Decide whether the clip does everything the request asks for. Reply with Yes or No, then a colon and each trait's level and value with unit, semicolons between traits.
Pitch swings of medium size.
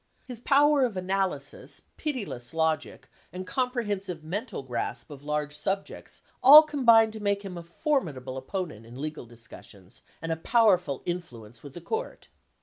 No: wide, 7.7 semitones